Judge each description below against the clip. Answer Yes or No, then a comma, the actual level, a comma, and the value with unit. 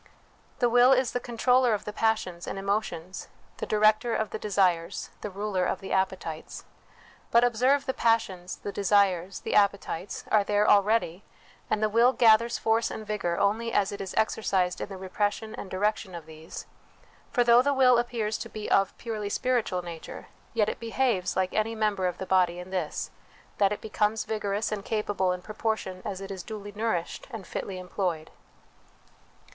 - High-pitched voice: Yes, high, 205 Hz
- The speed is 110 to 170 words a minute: No, average, 180 wpm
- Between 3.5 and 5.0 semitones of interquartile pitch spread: No, average, 3.1 semitones